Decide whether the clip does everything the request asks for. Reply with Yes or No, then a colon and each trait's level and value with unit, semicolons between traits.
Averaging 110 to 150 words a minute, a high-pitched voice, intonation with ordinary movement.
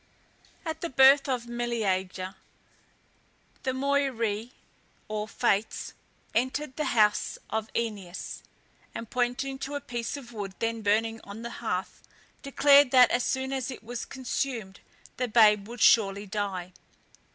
Yes: slow, 135 wpm; high, 235 Hz; average, 3.9 semitones